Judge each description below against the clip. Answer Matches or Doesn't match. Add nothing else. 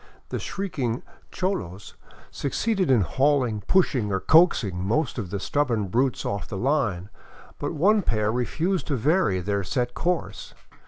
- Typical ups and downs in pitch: Doesn't match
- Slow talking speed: Doesn't match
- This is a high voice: Doesn't match